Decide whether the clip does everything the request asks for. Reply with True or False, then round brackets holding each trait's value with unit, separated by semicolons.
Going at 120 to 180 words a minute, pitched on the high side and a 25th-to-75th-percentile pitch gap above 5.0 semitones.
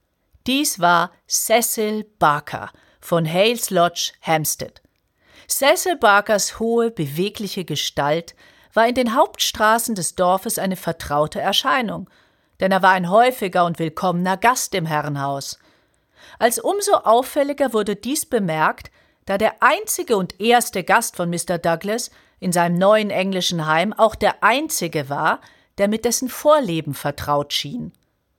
True (130 wpm; 200 Hz; 5.4 semitones)